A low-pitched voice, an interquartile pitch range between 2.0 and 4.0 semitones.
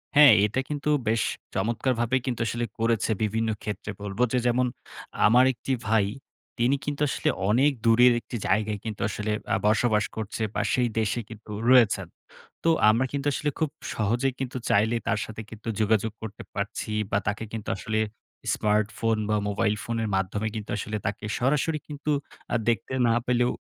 Yes: low, 115 Hz; average, 2.8 semitones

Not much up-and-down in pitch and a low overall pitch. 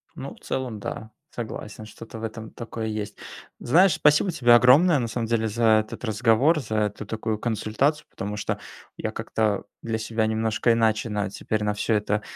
Yes: narrow, 1.9 semitones; low, 110 Hz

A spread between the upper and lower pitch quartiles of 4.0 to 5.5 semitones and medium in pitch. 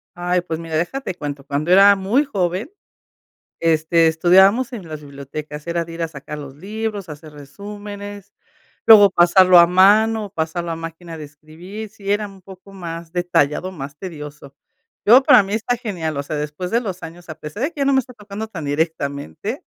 Yes: average, 4.6 semitones; medium, 175 Hz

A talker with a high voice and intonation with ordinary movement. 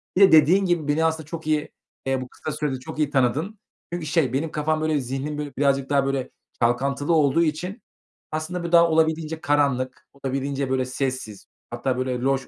No: medium, 145 Hz; average, 3.1 semitones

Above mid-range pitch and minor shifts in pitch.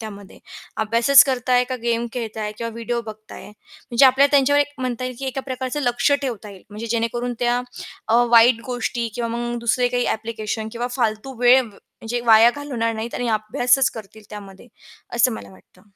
Yes: high, 240 Hz; narrow, 2.3 semitones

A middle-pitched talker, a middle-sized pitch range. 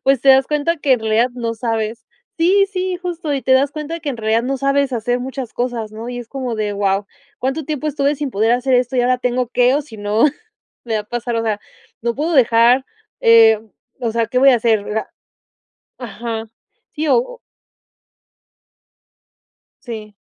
No: high, 245 Hz; average, 3.4 semitones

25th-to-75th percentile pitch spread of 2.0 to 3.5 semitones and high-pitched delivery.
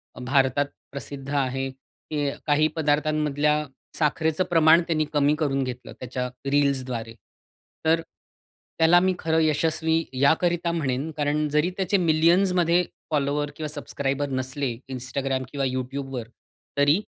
No: average, 2.9 semitones; medium, 145 Hz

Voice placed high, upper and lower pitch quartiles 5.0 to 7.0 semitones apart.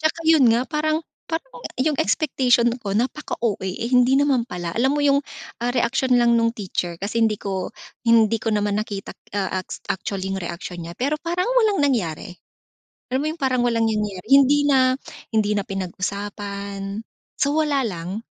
Yes: high, 230 Hz; wide, 5.5 semitones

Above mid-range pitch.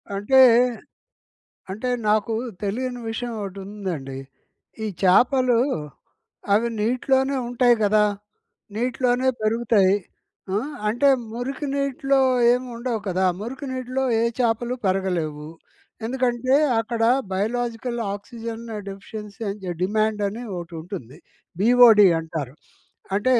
Yes: high, 225 Hz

